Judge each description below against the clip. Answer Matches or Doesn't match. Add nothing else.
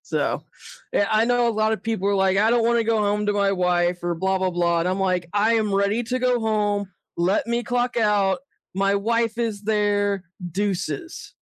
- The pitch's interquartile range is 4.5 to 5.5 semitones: Doesn't match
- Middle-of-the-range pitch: Doesn't match